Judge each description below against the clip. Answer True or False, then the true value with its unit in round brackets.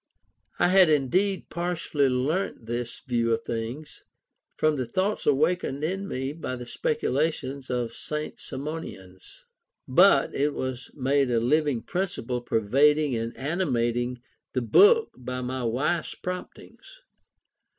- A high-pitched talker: False (135 Hz)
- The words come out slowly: True (130 wpm)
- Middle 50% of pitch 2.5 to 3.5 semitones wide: False (5.0 semitones)